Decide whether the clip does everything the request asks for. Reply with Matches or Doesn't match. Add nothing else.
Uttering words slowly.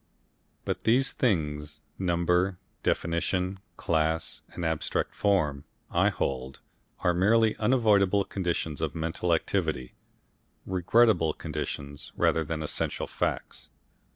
Matches